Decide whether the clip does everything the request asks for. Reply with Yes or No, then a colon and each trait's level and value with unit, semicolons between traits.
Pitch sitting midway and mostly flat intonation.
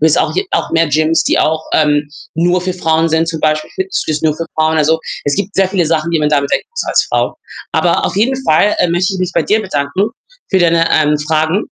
No: medium, 165 Hz; average, 3.1 semitones